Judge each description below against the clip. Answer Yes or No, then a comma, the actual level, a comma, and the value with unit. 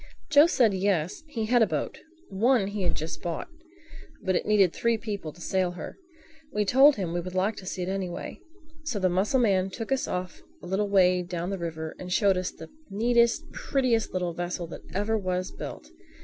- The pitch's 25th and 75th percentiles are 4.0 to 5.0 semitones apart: Yes, average, 4.3 semitones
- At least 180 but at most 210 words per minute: Yes, average, 195 wpm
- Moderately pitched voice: No, high, 195 Hz